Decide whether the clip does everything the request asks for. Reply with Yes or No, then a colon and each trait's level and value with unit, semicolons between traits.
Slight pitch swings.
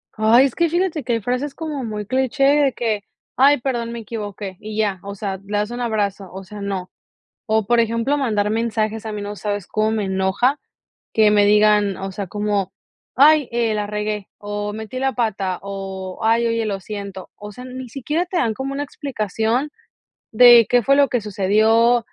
No: average, 3.3 semitones